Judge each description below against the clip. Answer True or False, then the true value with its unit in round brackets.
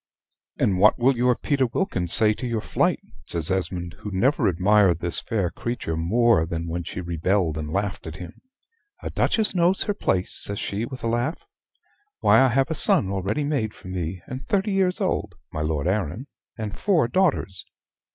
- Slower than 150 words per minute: False (185 wpm)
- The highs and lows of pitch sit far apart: True (6.8 semitones)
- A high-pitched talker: False (105 Hz)